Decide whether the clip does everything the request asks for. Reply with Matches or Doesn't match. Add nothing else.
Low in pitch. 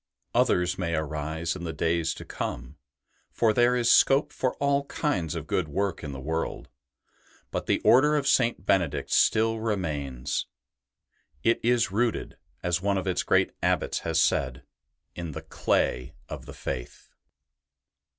Matches